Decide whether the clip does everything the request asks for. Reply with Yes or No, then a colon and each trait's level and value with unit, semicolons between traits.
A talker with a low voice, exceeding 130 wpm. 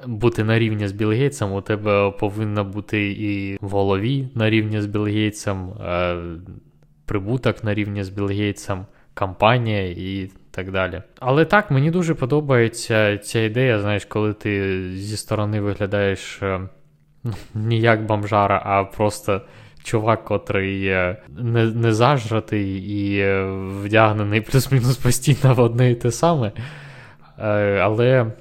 No: low, 105 Hz; average, 125 wpm